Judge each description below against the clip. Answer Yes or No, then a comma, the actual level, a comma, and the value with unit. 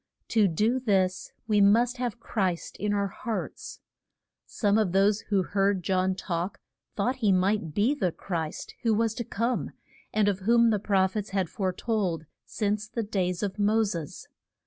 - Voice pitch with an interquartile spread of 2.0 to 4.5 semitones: Yes, average, 2.8 semitones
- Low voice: No, high, 205 Hz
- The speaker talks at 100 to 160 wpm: No, average, 175 wpm